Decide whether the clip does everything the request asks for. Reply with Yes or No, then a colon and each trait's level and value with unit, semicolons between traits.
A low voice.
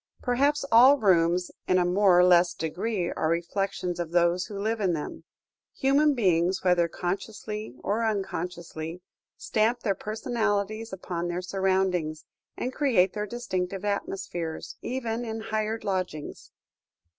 No: high, 190 Hz